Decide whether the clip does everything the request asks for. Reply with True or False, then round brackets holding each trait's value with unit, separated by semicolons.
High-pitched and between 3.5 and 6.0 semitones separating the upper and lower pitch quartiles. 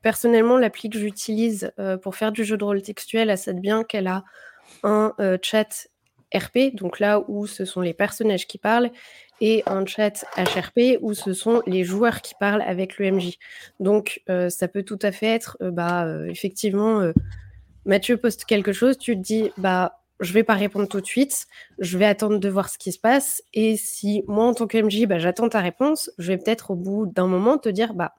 False (210 Hz; 3.0 semitones)